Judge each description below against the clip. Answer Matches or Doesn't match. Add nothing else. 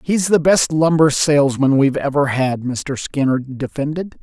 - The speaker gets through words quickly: Doesn't match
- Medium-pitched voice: Matches